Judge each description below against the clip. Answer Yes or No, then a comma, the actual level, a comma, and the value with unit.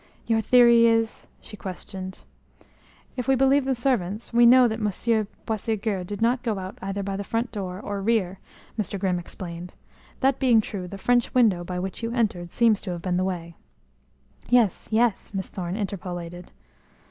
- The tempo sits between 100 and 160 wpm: No, average, 180 wpm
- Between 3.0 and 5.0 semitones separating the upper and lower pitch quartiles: Yes, average, 4.1 semitones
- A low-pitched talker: No, high, 205 Hz